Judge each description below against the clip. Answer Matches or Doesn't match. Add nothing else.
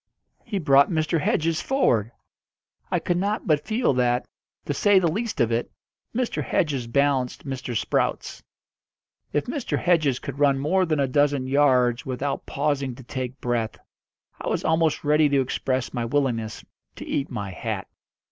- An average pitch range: Matches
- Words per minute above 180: Doesn't match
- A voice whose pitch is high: Doesn't match